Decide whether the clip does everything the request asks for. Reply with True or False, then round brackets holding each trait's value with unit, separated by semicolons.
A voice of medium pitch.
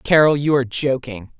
True (150 Hz)